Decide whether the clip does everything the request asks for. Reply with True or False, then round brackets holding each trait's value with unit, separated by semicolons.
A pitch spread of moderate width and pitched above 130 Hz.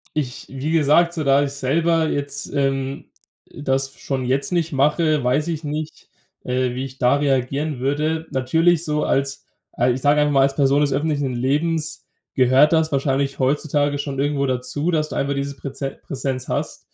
False (2.2 semitones; 140 Hz)